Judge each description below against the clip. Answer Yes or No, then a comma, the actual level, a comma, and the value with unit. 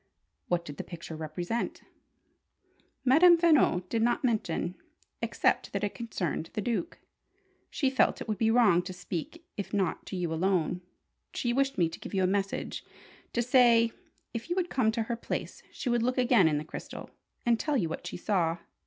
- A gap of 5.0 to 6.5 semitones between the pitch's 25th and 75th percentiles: Yes, wide, 5.6 semitones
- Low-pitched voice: No, high, 220 Hz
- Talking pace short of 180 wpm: No, average, 190 wpm